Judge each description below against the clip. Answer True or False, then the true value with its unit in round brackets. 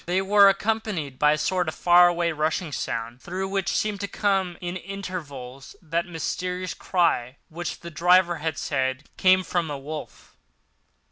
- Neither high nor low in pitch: True (175 Hz)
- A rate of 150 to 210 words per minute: True (160 wpm)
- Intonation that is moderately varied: True (3.7 semitones)